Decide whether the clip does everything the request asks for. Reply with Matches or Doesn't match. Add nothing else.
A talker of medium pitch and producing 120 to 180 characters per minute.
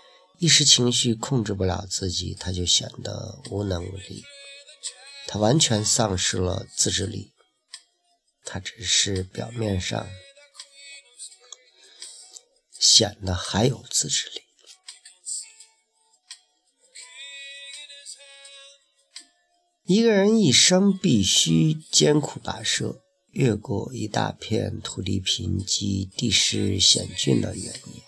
Matches